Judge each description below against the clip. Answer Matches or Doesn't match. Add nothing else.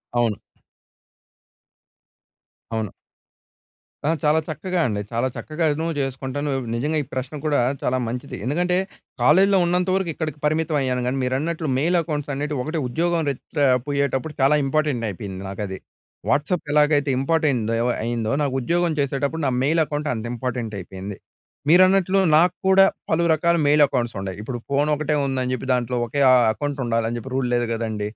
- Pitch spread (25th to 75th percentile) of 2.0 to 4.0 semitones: Doesn't match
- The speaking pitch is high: Doesn't match